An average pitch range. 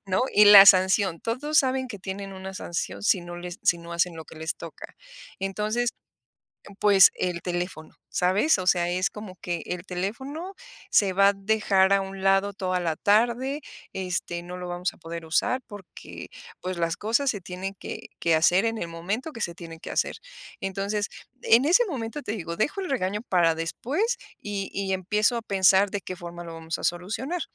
Yes: average, 3.5 semitones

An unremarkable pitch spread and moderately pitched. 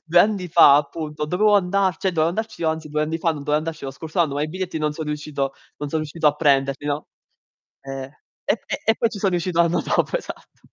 Yes: average, 3.3 semitones; medium, 160 Hz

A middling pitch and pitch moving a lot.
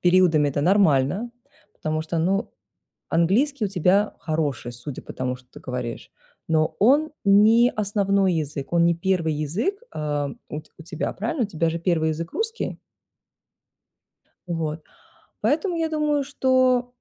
Yes: medium, 175 Hz; wide, 6.9 semitones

